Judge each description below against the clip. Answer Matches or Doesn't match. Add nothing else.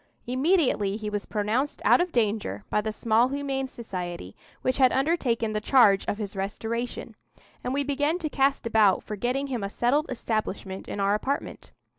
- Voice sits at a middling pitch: Doesn't match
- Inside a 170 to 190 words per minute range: Matches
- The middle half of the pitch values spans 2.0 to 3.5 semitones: Doesn't match